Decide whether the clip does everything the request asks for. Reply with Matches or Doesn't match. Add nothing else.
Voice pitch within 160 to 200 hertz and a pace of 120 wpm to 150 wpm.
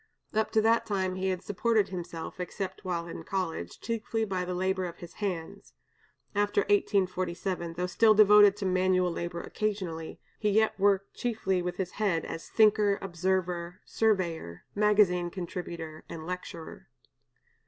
Matches